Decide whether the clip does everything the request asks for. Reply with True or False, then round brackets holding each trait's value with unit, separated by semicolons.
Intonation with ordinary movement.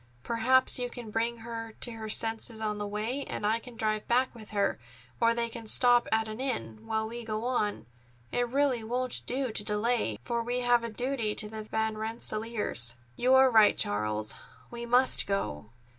False (2.2 semitones)